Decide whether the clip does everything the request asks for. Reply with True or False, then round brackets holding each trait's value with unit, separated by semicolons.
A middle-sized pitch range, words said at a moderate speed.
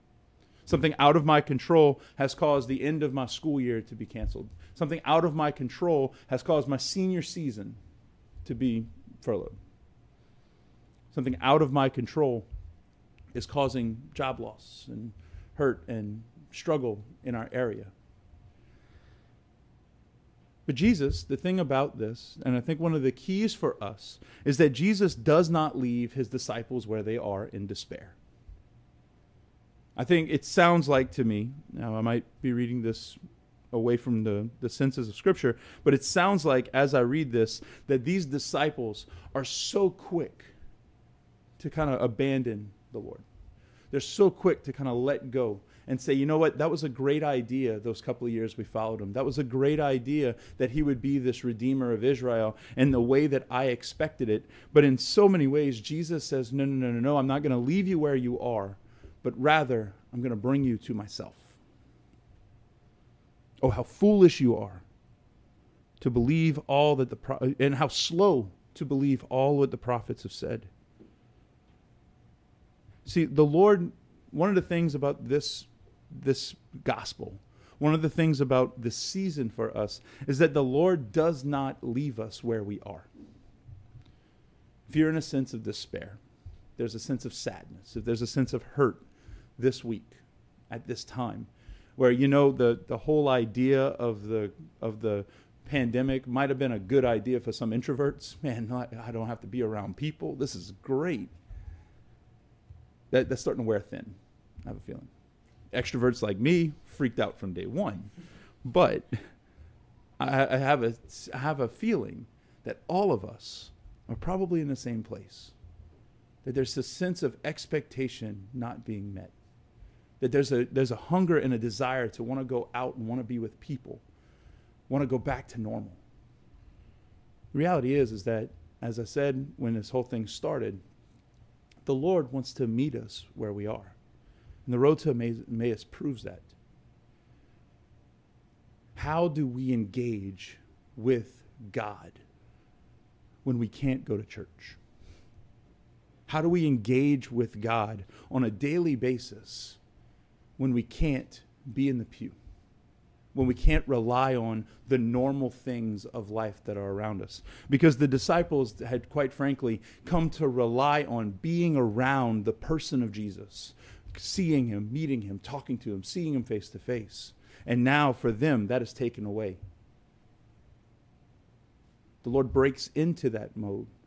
True (3.9 semitones; 165 wpm)